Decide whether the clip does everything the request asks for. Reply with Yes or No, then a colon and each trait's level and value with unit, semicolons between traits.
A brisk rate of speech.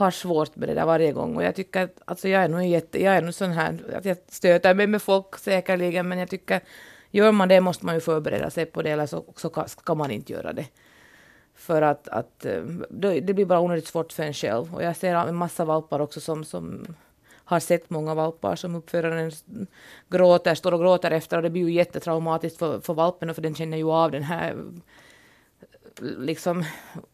Yes: fast, 210 wpm